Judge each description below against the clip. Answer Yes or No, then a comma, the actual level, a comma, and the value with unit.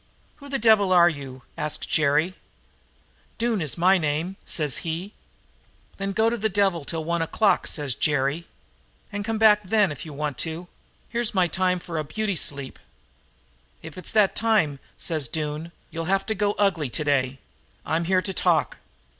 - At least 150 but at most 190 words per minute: Yes, average, 170 wpm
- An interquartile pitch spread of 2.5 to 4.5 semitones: No, average, 5.1 semitones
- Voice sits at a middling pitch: Yes, medium, 175 Hz